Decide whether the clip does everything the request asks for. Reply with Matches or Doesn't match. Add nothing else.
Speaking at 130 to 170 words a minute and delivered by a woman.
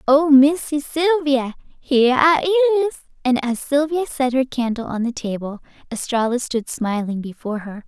Matches